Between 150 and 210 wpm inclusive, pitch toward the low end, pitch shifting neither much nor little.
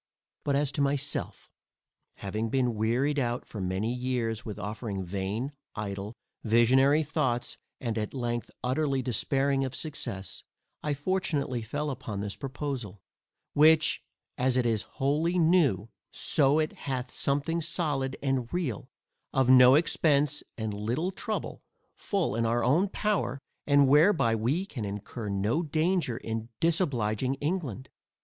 No: slow, 135 wpm; low, 130 Hz; average, 4.7 semitones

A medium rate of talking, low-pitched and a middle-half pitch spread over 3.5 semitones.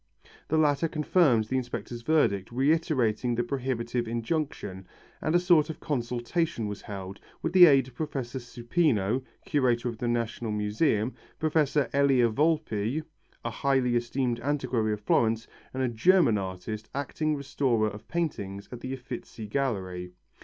Yes: average, 145 wpm; low, 125 Hz; average, 4.7 semitones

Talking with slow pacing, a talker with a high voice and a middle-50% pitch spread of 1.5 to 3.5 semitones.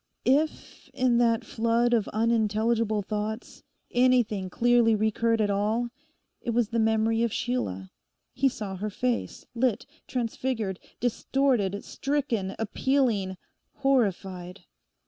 Yes: slow, 110 wpm; high, 225 Hz; average, 2.7 semitones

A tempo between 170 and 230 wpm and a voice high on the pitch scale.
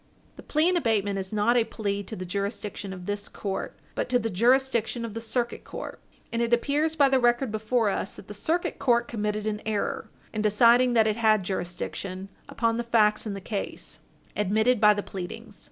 Yes: average, 200 wpm; high, 220 Hz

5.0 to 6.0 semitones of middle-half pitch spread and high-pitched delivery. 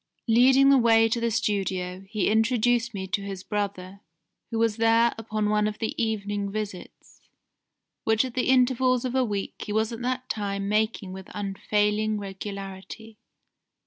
No: narrow, 2.6 semitones; high, 215 Hz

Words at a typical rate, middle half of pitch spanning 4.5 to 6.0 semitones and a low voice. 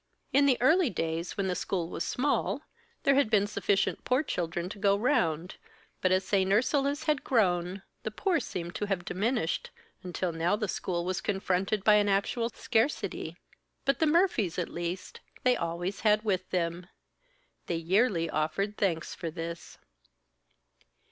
No: average, 160 wpm; average, 4.9 semitones; high, 195 Hz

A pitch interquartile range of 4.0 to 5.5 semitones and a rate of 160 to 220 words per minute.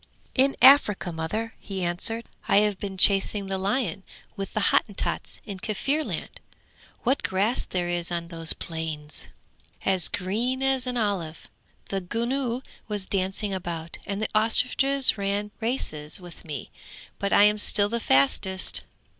No: average, 4.4 semitones; average, 145 wpm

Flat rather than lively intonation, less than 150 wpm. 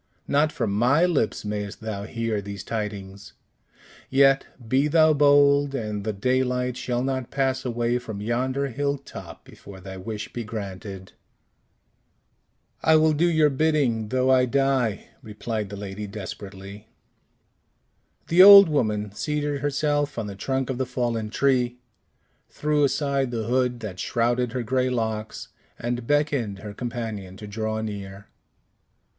No: average, 4.6 semitones; average, 140 wpm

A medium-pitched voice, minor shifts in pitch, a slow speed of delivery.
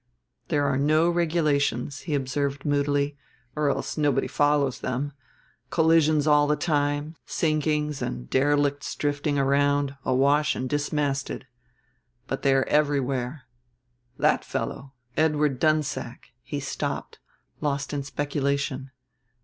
Yes: medium, 145 Hz; narrow, 1.4 semitones; slow, 115 wpm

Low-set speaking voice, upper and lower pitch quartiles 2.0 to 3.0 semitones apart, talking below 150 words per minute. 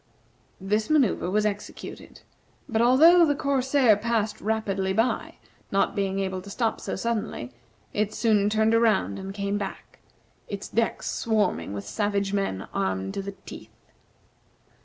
No: high, 210 Hz; average, 2.7 semitones; average, 140 wpm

